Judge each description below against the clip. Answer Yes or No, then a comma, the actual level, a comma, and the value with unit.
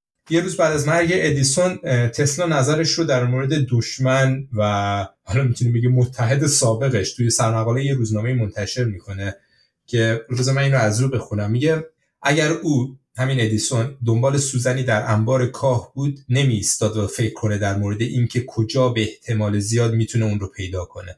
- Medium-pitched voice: No, low, 125 Hz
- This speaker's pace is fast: Yes, fast, 165 wpm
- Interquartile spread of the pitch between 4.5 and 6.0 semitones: No, average, 3.6 semitones